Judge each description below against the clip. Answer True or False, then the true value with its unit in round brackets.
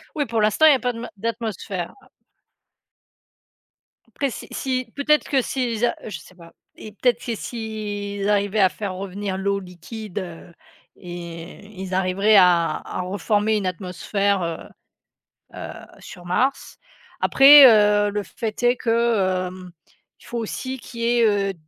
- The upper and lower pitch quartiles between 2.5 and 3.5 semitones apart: False (3.9 semitones)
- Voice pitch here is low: False (205 Hz)